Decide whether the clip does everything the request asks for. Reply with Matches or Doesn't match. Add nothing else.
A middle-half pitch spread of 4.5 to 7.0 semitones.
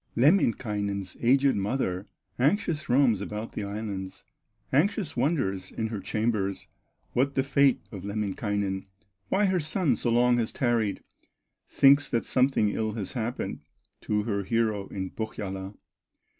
Matches